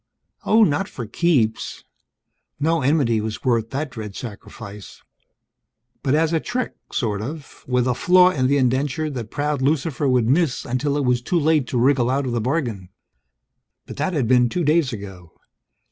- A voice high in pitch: No, low, 130 Hz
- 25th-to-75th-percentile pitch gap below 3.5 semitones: No, average, 4.4 semitones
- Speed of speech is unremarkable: Yes, average, 175 wpm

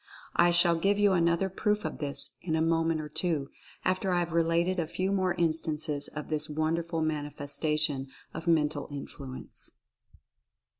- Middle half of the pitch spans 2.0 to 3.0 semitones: Yes, narrow, 2.4 semitones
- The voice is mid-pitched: Yes, medium, 165 Hz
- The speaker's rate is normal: Yes, average, 160 wpm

